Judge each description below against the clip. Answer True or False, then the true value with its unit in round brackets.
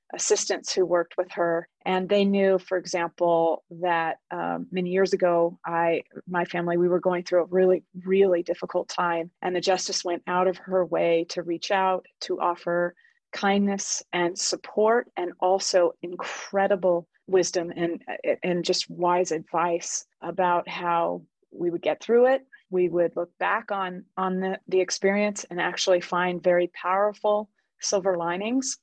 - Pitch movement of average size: False (2.1 semitones)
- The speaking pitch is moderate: True (180 Hz)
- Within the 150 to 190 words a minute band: True (155 wpm)